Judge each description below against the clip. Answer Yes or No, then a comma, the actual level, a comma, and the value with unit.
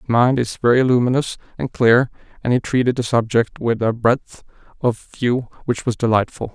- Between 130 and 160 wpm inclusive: No, average, 185 wpm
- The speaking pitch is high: No, low, 120 Hz